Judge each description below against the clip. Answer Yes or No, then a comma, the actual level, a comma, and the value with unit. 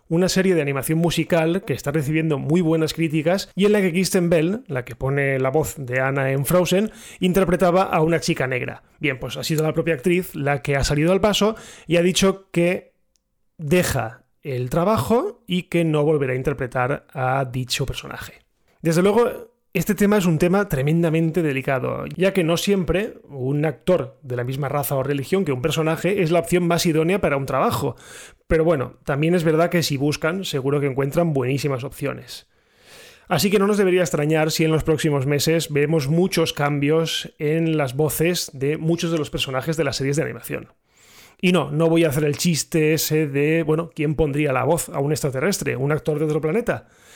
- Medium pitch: Yes, medium, 160 Hz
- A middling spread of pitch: Yes, average, 3.7 semitones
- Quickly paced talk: Yes, fast, 195 wpm